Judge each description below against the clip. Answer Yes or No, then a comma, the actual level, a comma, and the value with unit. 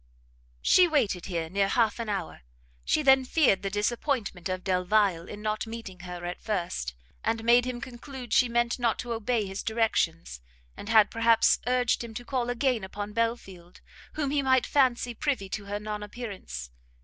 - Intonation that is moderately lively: Yes, average, 3.9 semitones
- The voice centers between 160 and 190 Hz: No, high, 225 Hz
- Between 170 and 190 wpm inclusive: Yes, average, 175 wpm